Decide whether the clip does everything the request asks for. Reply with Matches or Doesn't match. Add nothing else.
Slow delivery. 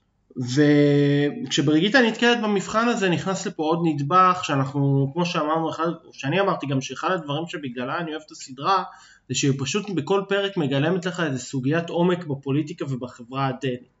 Doesn't match